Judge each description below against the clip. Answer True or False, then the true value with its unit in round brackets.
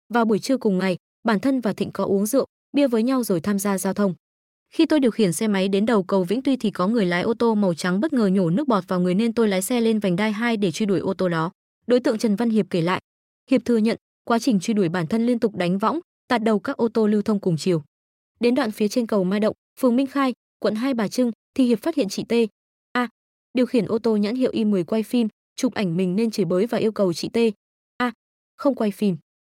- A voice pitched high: True (220 Hz)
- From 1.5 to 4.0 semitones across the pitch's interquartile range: True (3.6 semitones)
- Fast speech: True (275 wpm)